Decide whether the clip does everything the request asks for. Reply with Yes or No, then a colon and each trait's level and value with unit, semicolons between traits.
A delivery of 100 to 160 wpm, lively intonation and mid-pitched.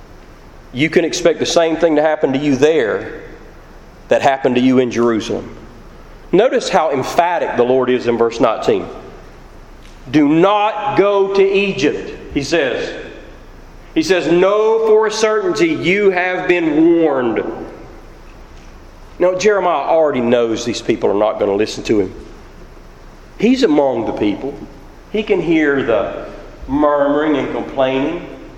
Yes: average, 140 wpm; wide, 7.1 semitones; medium, 165 Hz